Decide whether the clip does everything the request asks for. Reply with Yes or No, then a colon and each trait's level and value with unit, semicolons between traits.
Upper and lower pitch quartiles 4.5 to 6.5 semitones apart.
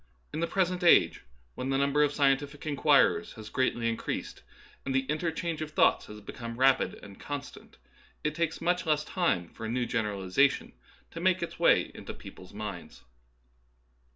Yes: average, 5.1 semitones